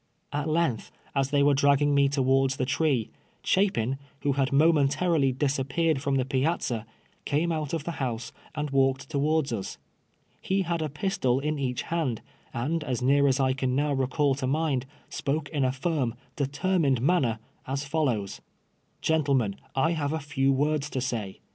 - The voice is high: No, medium, 140 Hz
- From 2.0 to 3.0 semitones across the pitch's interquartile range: Yes, average, 2.7 semitones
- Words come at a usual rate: Yes, average, 170 wpm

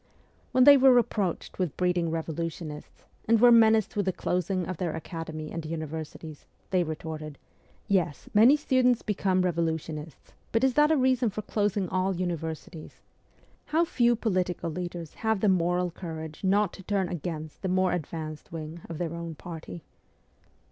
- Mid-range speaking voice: Yes, medium, 180 Hz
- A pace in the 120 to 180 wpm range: Yes, average, 160 wpm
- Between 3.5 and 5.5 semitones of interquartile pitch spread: Yes, average, 4.3 semitones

